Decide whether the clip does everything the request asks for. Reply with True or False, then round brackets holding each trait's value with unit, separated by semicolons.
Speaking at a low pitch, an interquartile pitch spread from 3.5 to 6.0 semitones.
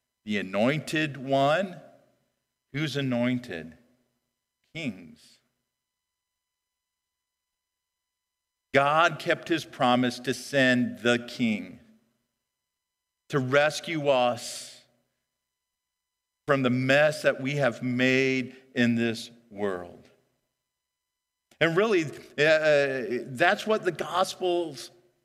True (125 Hz; 4.8 semitones)